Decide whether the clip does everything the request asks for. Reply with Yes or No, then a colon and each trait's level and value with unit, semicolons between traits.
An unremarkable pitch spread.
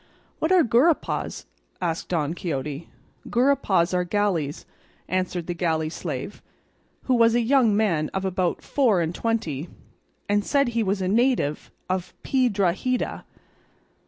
No: wide, 5.7 semitones